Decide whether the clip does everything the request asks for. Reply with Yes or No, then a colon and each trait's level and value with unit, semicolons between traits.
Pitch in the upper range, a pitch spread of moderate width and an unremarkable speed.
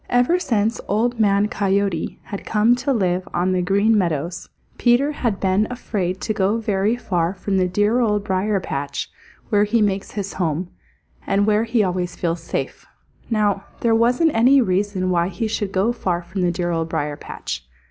Yes: high, 200 Hz; average, 3.6 semitones; average, 180 wpm